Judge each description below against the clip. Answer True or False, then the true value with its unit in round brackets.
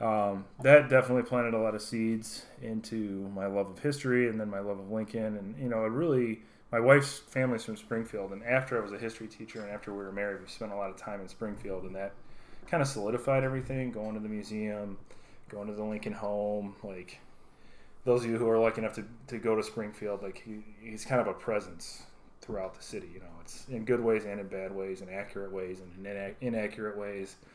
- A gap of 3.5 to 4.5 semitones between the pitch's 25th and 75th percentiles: False (2.5 semitones)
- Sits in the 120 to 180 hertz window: False (110 Hz)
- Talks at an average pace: False (225 wpm)